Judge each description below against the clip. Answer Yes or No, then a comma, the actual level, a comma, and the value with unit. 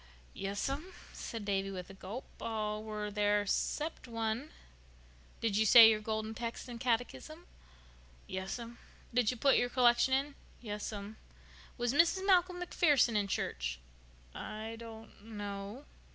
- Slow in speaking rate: Yes, slow, 130 wpm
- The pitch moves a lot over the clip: No, average, 3.4 semitones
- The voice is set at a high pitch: Yes, high, 225 Hz